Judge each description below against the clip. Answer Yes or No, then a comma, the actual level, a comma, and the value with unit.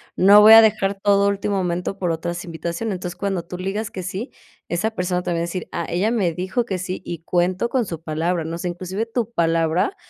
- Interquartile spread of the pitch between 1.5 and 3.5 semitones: Yes, average, 2.9 semitones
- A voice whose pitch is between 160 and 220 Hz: Yes, medium, 185 Hz